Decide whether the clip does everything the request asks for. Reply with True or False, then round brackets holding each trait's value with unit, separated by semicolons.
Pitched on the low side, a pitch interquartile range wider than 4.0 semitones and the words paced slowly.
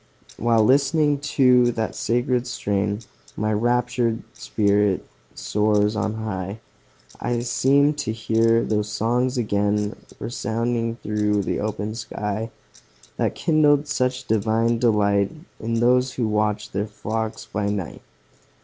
False (110 Hz; 2.7 semitones; 120 wpm)